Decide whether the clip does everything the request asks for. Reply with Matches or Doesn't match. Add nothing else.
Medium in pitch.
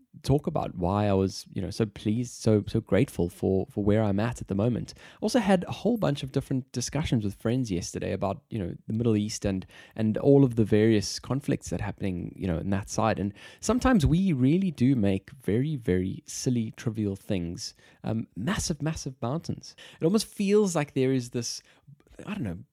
Doesn't match